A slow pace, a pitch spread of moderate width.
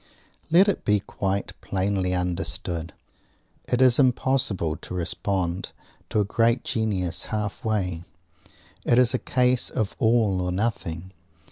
Yes: slow, 125 wpm; average, 4.4 semitones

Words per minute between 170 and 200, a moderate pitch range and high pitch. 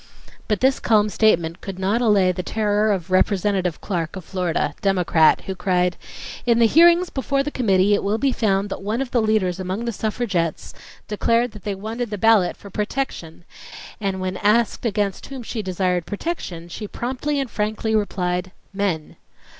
Yes: average, 180 wpm; average, 3.6 semitones; high, 205 Hz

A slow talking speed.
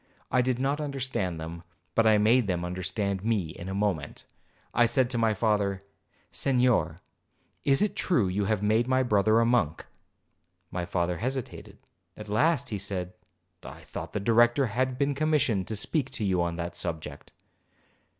No: average, 170 wpm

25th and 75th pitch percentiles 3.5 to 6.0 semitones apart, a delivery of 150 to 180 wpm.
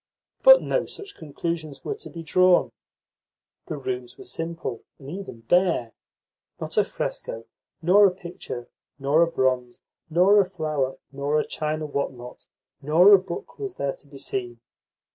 Yes: average, 5.3 semitones; average, 160 wpm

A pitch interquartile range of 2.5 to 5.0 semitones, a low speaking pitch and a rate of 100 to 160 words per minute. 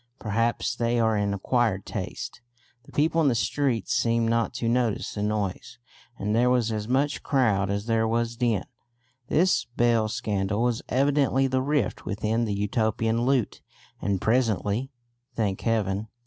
Yes: average, 2.9 semitones; low, 115 Hz; average, 155 wpm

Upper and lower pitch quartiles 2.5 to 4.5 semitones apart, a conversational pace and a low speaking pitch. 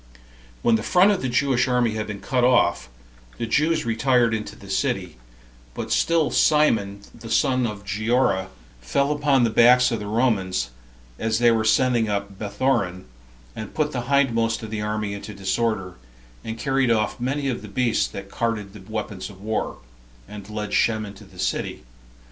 Yes: average, 3.3 semitones; average, 175 wpm; low, 115 Hz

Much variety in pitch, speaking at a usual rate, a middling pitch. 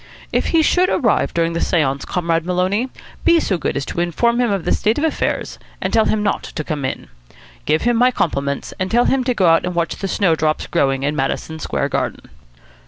No: wide, 6.7 semitones; fast, 220 wpm; medium, 180 Hz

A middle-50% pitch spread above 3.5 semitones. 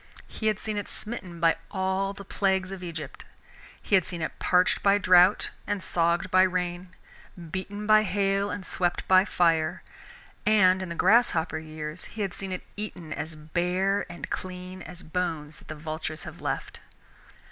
No: average, 2.7 semitones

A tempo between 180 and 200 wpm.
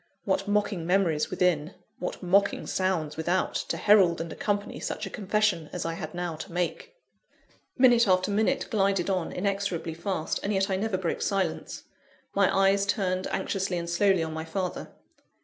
No: average, 165 wpm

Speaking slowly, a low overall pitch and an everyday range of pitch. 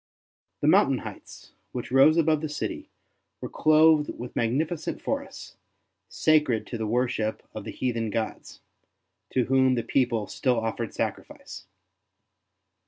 Yes: slow, 130 wpm; low, 125 Hz; average, 4.7 semitones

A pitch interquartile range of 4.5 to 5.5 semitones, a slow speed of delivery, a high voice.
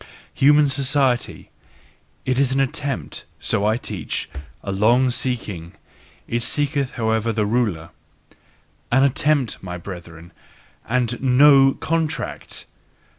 No: average, 4.9 semitones; slow, 110 wpm; low, 125 Hz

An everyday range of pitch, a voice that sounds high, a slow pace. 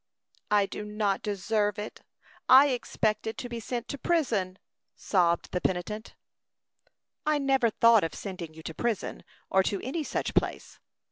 No: average, 4.0 semitones; high, 210 Hz; average, 150 wpm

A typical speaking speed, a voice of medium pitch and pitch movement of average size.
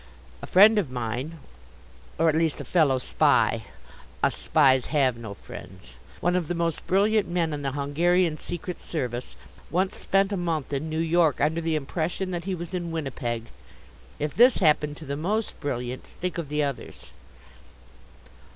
Yes: average, 170 wpm; medium, 160 Hz; average, 4.0 semitones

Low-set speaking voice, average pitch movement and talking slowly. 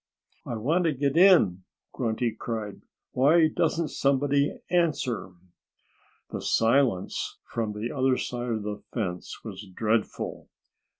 Yes: low, 120 Hz; average, 5.0 semitones; slow, 120 wpm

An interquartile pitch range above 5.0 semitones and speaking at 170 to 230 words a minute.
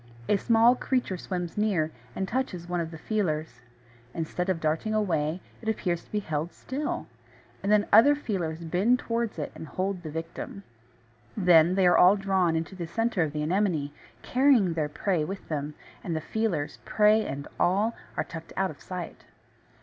No: average, 4.6 semitones; average, 180 wpm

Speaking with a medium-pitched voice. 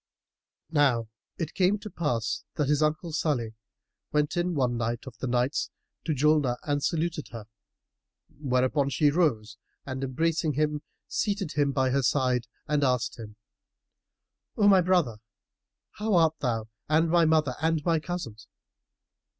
Yes: medium, 145 Hz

